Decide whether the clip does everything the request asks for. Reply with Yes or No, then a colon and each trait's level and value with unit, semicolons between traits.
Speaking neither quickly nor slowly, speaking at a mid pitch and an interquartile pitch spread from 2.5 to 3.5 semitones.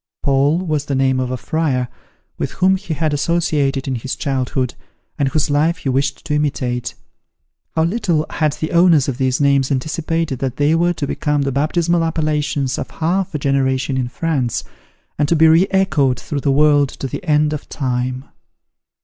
Yes: average, 185 wpm; medium, 145 Hz; average, 3.2 semitones